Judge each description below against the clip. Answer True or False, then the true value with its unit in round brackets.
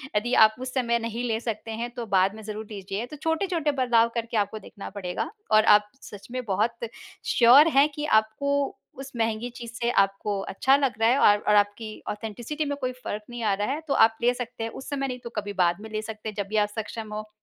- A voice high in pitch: True (225 Hz)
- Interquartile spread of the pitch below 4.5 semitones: True (2.8 semitones)